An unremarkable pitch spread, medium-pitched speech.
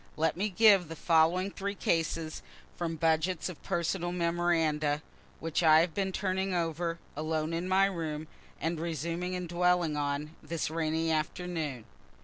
No: narrow, 2.1 semitones; medium, 165 Hz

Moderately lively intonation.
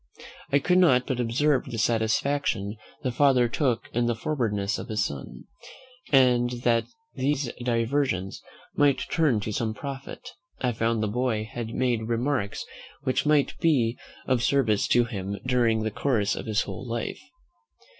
Yes: average, 3.4 semitones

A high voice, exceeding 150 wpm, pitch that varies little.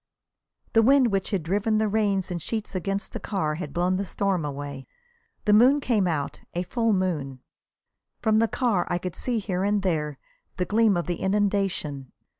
No: high, 195 Hz; average, 185 wpm; average, 3.9 semitones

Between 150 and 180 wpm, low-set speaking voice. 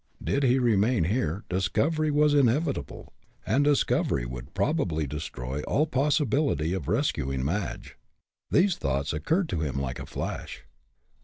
No: slow, 135 wpm; low, 100 Hz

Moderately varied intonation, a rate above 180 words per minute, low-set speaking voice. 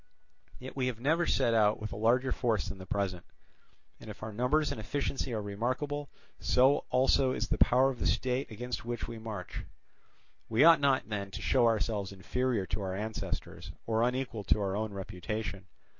Yes: average, 3.9 semitones; average, 190 wpm; low, 115 Hz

